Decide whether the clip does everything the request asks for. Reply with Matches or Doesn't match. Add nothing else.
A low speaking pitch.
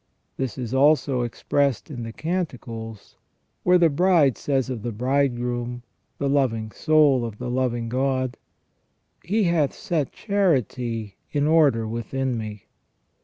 Matches